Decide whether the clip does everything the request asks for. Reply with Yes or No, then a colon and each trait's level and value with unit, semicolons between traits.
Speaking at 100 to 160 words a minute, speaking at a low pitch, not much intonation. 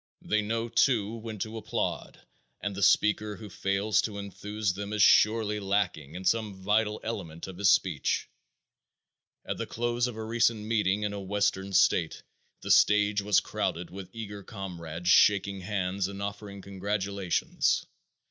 Yes: average, 155 wpm; low, 100 Hz; narrow, 1.9 semitones